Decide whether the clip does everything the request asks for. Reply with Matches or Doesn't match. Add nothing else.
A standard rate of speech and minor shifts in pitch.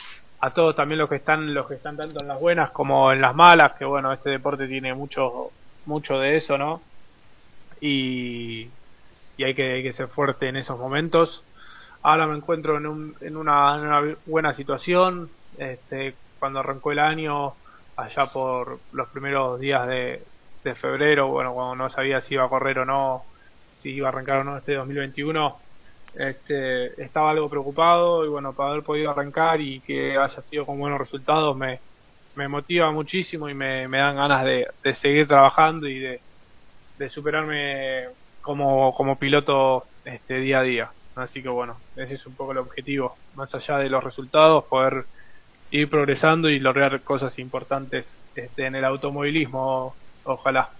Matches